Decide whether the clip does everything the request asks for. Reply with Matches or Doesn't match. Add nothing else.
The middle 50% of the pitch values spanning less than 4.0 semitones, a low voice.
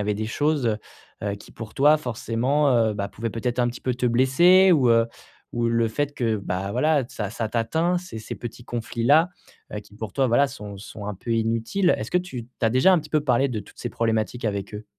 Doesn't match